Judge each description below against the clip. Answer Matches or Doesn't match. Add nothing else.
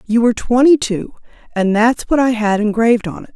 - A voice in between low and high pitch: Doesn't match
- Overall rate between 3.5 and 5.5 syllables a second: Doesn't match